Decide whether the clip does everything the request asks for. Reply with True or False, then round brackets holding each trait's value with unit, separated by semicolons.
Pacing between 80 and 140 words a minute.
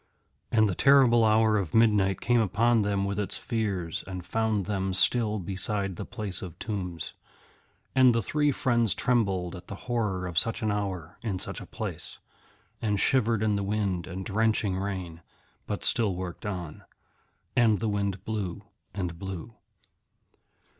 False (160 wpm)